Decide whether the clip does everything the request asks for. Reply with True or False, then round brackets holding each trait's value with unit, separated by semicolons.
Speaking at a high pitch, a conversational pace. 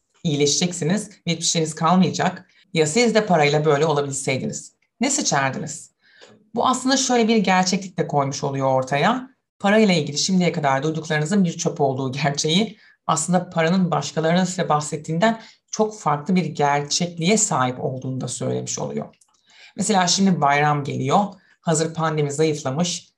False (160 Hz; 130 wpm)